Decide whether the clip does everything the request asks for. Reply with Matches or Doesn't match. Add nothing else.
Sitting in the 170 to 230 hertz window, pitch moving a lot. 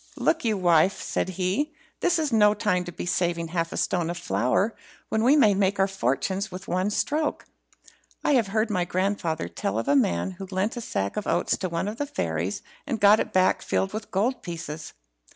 Doesn't match